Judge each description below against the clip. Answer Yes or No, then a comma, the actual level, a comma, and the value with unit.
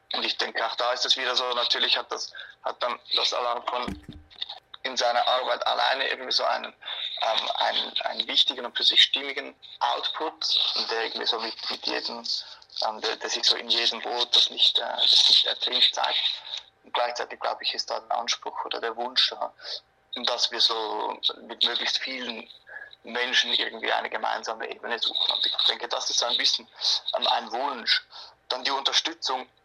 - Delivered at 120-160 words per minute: No, average, 185 wpm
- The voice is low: Yes, low, 125 Hz